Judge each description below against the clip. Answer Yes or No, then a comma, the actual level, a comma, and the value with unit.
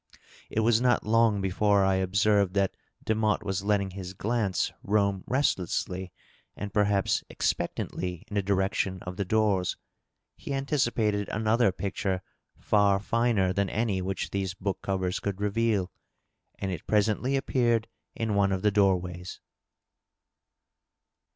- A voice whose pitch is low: Yes, low, 100 Hz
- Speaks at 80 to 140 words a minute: Yes, slow, 135 wpm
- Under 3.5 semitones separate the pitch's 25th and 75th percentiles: Yes, narrow, 2.4 semitones